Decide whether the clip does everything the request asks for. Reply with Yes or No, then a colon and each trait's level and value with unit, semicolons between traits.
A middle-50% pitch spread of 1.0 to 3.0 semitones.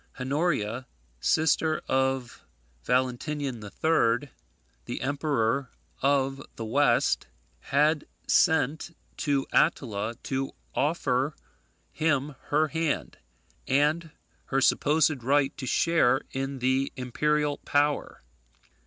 Yes: average, 2.7 semitones